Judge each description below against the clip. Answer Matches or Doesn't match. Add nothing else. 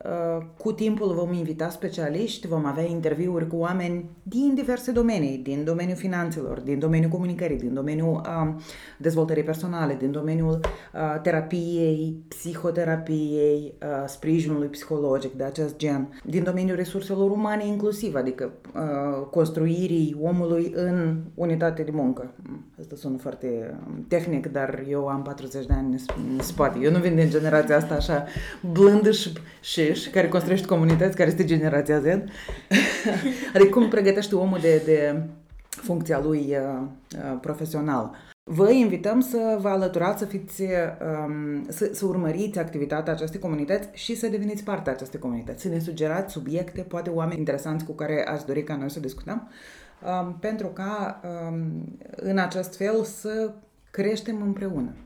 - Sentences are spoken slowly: Doesn't match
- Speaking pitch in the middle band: Matches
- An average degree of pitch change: Matches